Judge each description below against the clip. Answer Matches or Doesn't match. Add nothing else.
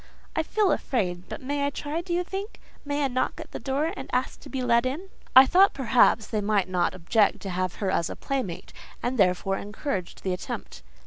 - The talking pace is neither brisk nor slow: Doesn't match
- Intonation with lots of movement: Matches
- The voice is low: Doesn't match